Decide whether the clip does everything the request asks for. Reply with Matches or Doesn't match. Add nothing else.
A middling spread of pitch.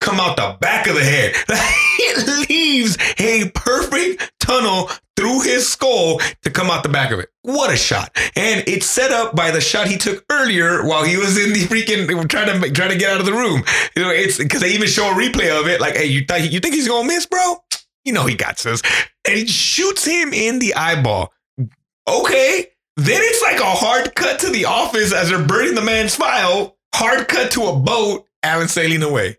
Doesn't match